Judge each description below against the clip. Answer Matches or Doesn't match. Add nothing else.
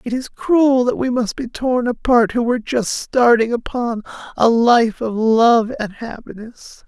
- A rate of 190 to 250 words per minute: Doesn't match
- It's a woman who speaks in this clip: Matches